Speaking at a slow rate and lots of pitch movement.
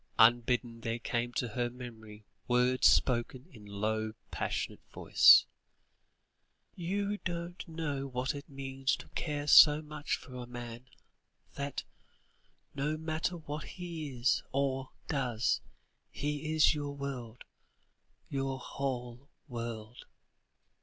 No: slow, 120 wpm; average, 3.6 semitones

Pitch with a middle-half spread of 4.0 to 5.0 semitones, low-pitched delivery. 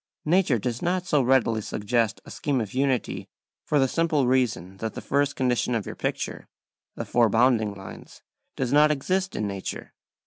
Yes: average, 4.5 semitones; low, 125 Hz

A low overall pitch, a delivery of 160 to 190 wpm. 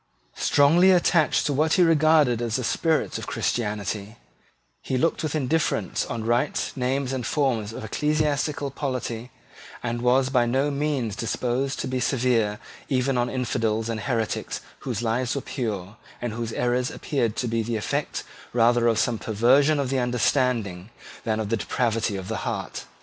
Yes: low, 125 Hz; average, 165 wpm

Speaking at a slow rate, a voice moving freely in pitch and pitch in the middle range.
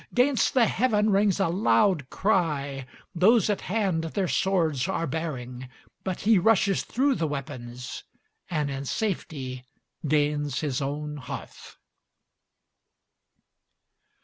Yes: slow, 115 wpm; wide, 6.3 semitones; medium, 165 Hz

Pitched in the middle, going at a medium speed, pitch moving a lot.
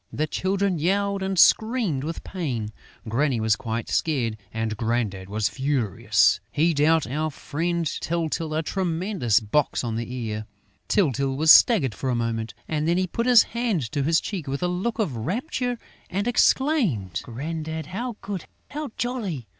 Yes: medium, 155 Hz; average, 160 wpm; wide, 8.1 semitones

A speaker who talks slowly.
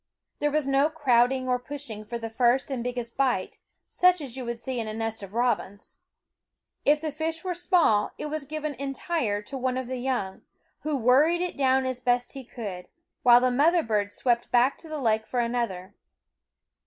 No: average, 195 wpm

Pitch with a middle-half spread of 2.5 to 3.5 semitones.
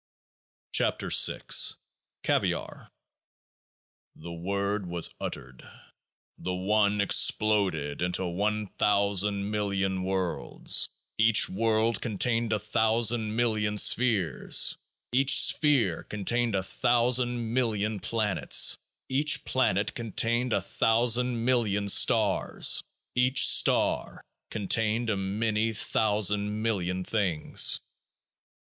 Yes: average, 2.9 semitones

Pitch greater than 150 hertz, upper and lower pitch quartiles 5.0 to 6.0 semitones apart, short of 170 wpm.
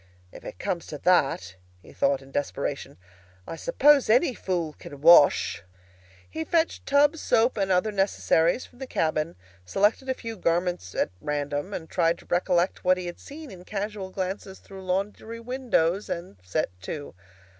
Yes: medium, 185 Hz; wide, 5.5 semitones; average, 160 wpm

